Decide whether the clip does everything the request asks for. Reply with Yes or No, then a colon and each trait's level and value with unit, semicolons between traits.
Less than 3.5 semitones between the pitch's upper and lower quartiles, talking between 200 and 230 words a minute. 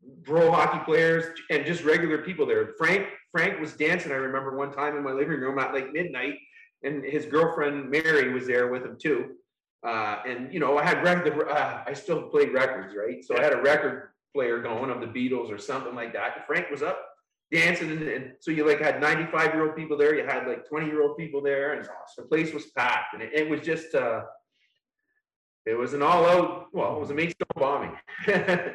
Yes: average, 2.8 semitones; fast, 205 wpm